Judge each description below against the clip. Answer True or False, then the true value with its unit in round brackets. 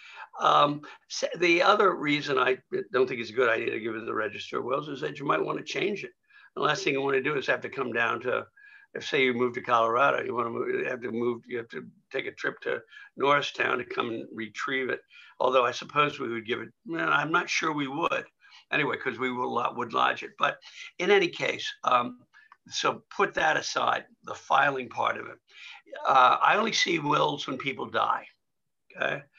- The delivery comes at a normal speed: False (225 wpm)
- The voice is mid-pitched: True (175 Hz)